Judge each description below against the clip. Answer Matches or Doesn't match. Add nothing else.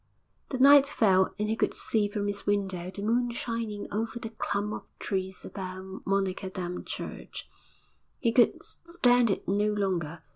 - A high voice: Matches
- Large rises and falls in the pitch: Doesn't match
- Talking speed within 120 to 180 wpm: Matches